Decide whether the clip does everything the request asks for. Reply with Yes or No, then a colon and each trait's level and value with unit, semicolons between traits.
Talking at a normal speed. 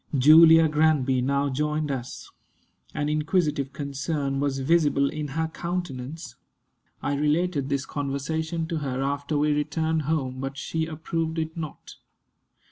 No: slow, 130 wpm